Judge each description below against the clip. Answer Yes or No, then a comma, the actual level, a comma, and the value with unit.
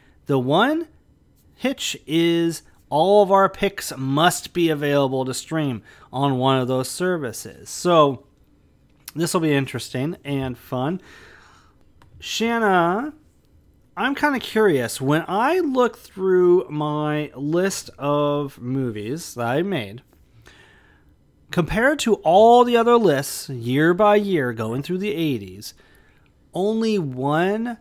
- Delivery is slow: Yes, slow, 120 wpm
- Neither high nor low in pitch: Yes, medium, 160 Hz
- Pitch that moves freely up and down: Yes, wide, 6.8 semitones